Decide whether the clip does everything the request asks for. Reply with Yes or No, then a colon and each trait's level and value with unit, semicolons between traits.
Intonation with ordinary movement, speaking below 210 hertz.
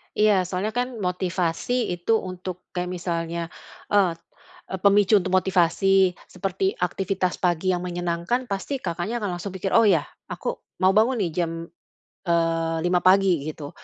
No: narrow, 2.1 semitones; medium, 185 Hz